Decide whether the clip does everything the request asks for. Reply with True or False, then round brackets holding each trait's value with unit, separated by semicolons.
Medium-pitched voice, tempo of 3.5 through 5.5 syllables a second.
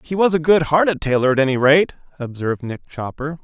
False (150 Hz; 6.0 syllables/s)